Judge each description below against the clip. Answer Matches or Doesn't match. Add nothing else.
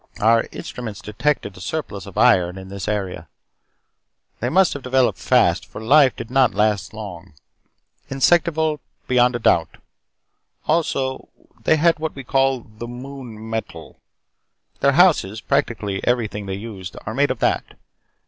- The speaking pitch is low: Matches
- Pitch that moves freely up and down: Doesn't match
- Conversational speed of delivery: Matches